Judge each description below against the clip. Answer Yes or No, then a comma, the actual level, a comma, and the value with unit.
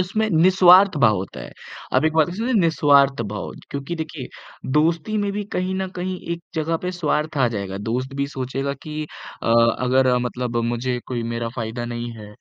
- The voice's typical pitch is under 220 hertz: Yes, medium, 140 Hz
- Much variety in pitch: Yes, wide, 6.2 semitones